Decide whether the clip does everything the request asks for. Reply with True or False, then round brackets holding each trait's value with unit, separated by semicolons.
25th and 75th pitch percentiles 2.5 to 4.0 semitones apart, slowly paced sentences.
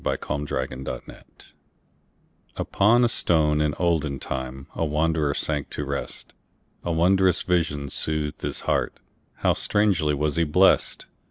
True (3.1 semitones; 120 wpm)